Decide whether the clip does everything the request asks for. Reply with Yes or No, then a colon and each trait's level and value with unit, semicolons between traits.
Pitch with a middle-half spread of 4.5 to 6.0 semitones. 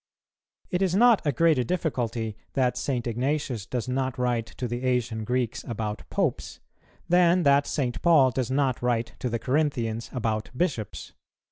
No: average, 3.8 semitones